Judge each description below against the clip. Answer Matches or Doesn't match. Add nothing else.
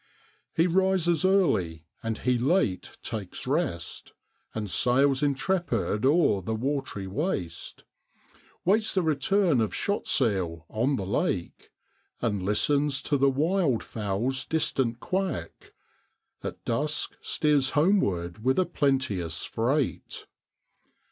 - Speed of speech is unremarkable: Doesn't match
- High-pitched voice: Doesn't match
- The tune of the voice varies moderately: Doesn't match